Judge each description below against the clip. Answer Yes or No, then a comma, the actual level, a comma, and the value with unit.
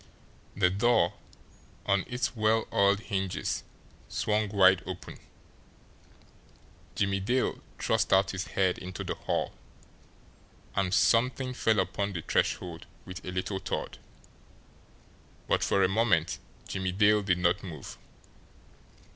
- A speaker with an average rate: No, slow, 120 wpm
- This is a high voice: No, low, 100 Hz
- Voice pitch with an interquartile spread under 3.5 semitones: Yes, narrow, 2.5 semitones